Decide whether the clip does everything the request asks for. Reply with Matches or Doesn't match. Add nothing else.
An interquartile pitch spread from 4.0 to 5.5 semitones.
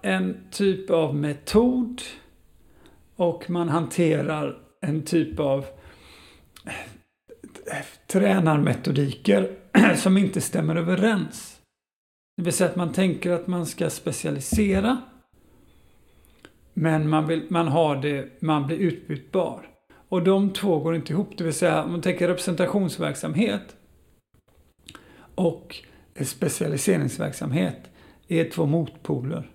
Doesn't match